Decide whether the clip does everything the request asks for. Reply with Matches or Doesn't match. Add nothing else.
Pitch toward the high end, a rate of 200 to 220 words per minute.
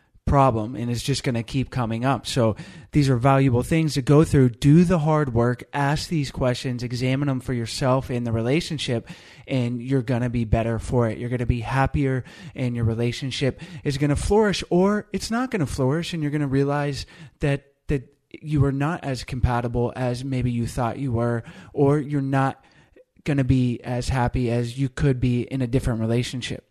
Doesn't match